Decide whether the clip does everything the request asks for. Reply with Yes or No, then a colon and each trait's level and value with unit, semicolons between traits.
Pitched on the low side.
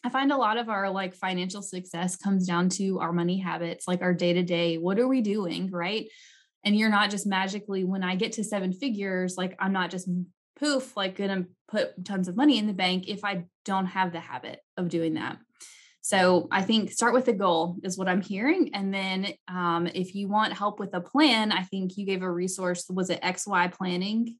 No: high, 190 Hz